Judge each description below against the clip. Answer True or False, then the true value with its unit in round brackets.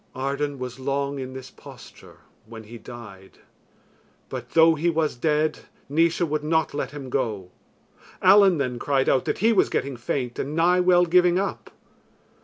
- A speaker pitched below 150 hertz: True (140 Hz)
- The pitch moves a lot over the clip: False (4.4 semitones)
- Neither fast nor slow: True (165 wpm)